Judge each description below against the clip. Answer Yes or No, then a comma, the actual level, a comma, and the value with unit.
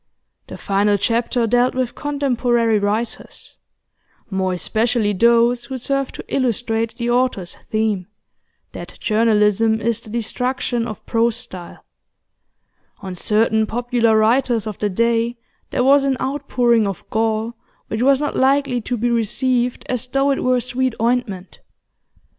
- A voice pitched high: Yes, high, 235 Hz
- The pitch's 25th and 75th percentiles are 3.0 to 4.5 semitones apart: No, narrow, 2.4 semitones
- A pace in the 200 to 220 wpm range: No, slow, 135 wpm